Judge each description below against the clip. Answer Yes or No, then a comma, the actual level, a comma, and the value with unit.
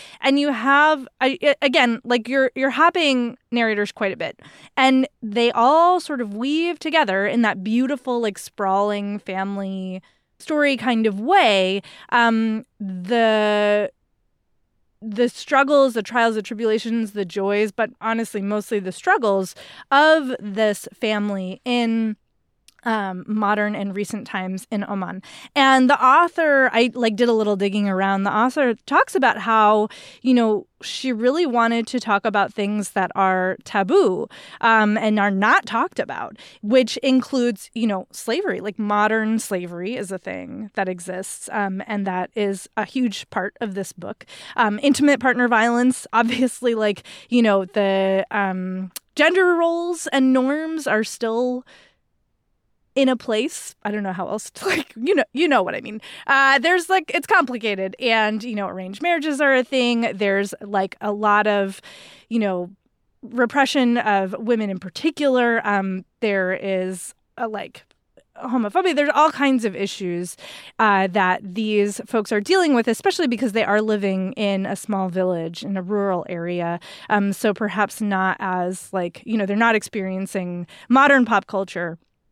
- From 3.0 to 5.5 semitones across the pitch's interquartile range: Yes, average, 4.4 semitones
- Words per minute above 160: No, average, 155 wpm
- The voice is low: No, high, 220 Hz